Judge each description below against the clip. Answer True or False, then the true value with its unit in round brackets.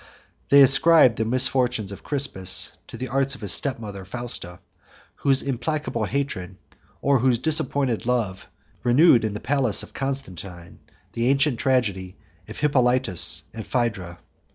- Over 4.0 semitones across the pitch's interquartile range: True (4.8 semitones)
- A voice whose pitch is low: True (125 Hz)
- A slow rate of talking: False (145 wpm)